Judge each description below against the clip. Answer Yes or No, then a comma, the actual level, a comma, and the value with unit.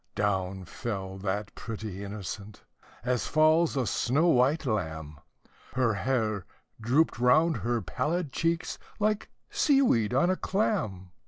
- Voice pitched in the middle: No, low, 120 Hz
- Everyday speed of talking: No, slow, 130 wpm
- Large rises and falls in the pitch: Yes, wide, 7.8 semitones